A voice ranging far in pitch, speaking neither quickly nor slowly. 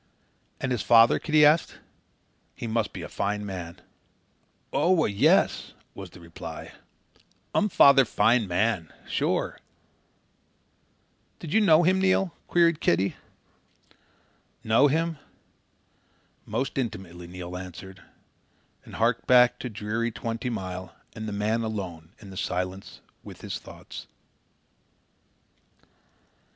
No: wide, 6.3 semitones; slow, 115 wpm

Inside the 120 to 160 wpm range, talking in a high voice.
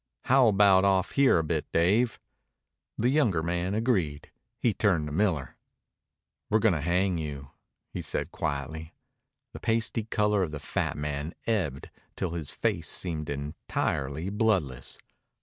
No: average, 145 wpm; very low, 90 Hz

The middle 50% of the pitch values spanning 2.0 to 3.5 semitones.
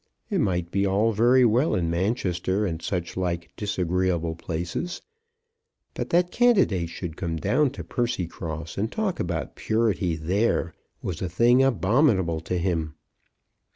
No: wide, 5.5 semitones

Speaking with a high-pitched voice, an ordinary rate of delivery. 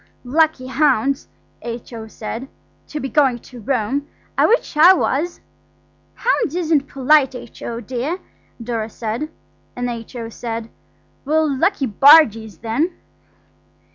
No: very high, 260 Hz; slow, 115 wpm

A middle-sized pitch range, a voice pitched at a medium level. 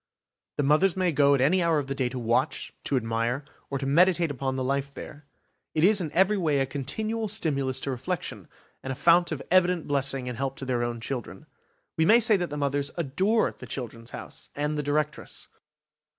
Yes: average, 4.5 semitones; medium, 145 Hz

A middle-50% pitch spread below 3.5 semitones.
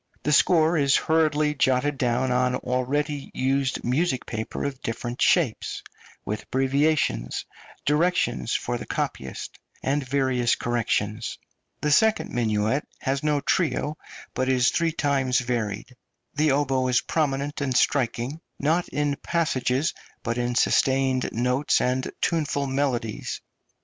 Yes: average, 2.9 semitones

